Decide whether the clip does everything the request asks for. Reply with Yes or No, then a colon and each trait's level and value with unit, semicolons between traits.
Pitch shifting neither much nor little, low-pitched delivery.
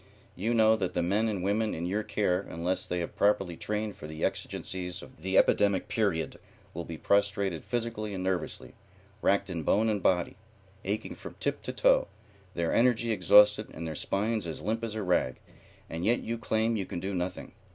Yes: average, 3.5 semitones; low, 100 Hz